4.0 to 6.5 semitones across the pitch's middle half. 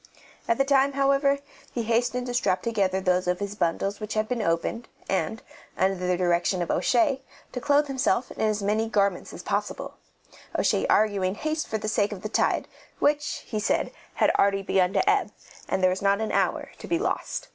Yes: average, 4.7 semitones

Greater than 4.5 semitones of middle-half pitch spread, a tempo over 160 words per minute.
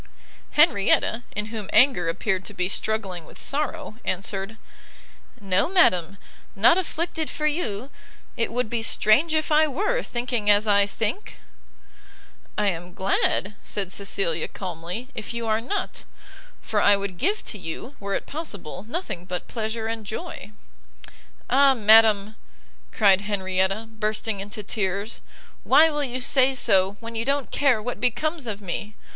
No: average, 5.0 semitones; average, 150 wpm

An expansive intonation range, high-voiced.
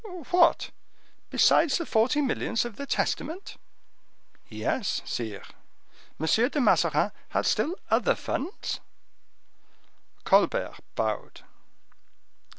Yes: wide, 6.4 semitones; very high, 270 Hz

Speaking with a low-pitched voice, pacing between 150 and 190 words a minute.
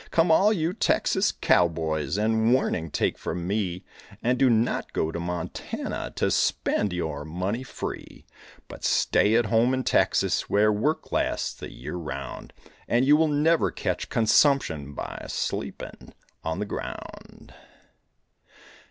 No: low, 105 Hz; average, 140 wpm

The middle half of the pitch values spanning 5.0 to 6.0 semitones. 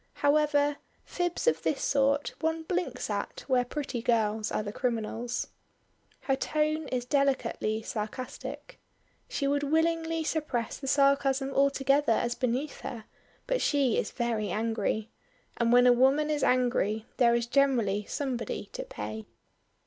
No: average, 3.9 semitones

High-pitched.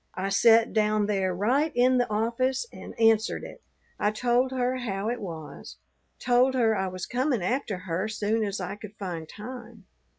Yes: high, 220 Hz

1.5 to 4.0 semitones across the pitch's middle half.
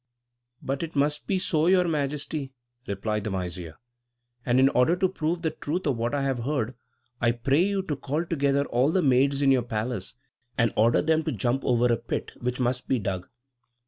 No: average, 4.5 semitones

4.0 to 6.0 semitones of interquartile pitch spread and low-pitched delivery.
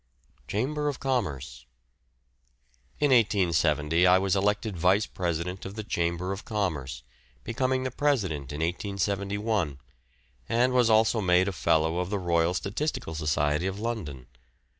Yes: average, 5.0 semitones; very low, 95 Hz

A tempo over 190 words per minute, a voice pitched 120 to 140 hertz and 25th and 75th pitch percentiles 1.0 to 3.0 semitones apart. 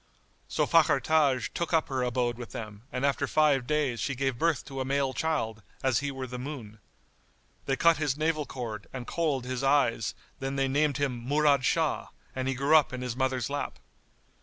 Yes: average, 200 wpm; low, 135 Hz; average, 2.7 semitones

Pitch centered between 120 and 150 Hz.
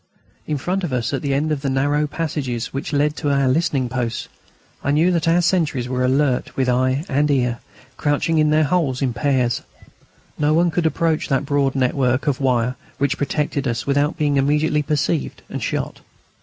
Yes: medium, 140 Hz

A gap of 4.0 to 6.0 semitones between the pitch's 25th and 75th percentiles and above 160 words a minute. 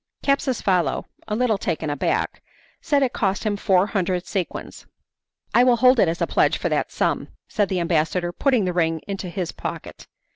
Yes: average, 5.0 semitones; average, 180 wpm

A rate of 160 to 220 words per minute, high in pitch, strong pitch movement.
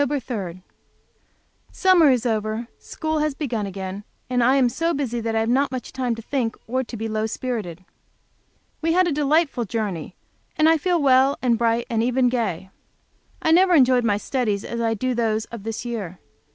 No: average, 185 wpm; high, 240 Hz; average, 4.0 semitones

